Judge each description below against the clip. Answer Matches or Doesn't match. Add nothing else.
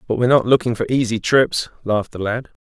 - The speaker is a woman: Doesn't match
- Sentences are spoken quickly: Matches